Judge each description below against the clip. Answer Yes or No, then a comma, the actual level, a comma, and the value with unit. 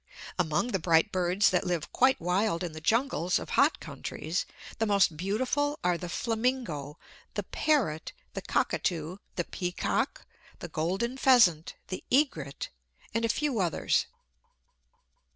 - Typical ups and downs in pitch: No, wide, 6.1 semitones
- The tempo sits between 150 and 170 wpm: No, slow, 135 wpm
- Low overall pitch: No, medium, 185 Hz